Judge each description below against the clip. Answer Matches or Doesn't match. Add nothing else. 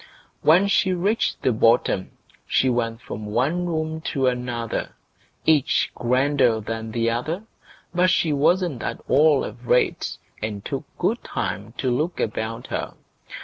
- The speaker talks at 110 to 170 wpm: Matches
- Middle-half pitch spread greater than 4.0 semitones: Matches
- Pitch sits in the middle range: Doesn't match